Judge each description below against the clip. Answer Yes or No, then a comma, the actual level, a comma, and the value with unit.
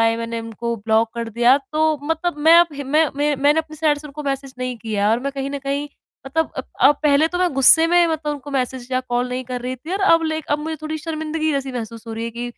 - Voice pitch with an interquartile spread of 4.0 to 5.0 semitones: Yes, average, 4.4 semitones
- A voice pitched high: Yes, very high, 275 Hz